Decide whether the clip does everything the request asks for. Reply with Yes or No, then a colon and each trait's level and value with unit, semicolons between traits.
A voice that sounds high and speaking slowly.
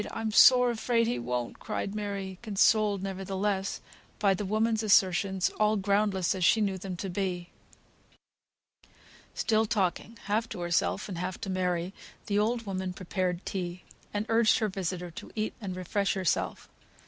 No: high, 195 Hz; average, 155 wpm